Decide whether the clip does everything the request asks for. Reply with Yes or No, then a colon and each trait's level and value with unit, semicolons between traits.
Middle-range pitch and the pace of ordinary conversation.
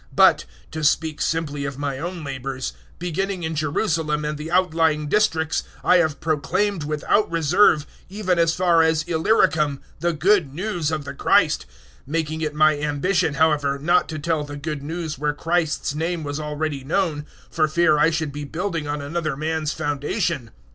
Yes: medium, 155 Hz; average, 170 wpm